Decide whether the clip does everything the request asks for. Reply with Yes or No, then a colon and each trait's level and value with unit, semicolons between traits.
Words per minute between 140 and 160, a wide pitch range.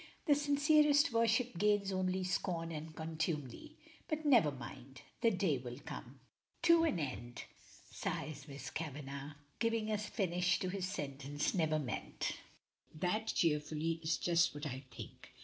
Yes: average, 145 wpm; wide, 6.4 semitones